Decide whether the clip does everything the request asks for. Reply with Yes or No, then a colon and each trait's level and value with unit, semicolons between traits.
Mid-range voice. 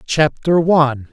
Yes: medium, 160 Hz